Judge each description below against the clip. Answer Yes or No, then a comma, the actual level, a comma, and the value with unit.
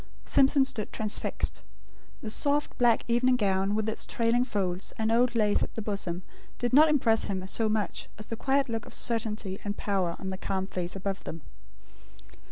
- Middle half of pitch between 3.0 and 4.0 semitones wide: Yes, average, 3.7 semitones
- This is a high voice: Yes, high, 215 Hz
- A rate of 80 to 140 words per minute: No, average, 180 wpm